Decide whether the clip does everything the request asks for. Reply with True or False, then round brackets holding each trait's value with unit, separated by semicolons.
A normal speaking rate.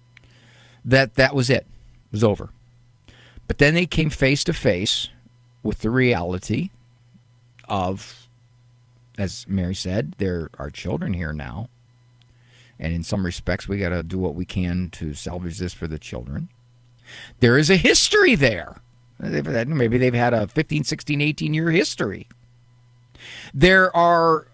True (145 wpm)